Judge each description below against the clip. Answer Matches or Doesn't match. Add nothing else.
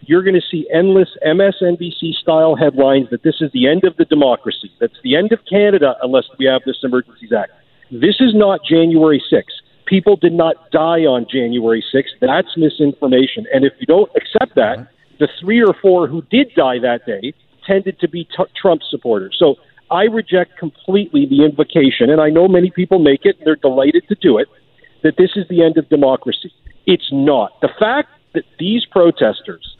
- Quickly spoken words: Doesn't match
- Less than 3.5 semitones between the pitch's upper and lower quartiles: Doesn't match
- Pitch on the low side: Doesn't match